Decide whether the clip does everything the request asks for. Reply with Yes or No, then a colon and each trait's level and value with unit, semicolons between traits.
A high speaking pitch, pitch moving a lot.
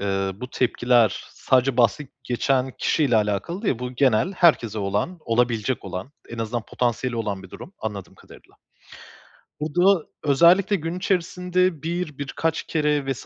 No: low, 130 Hz; wide, 6.5 semitones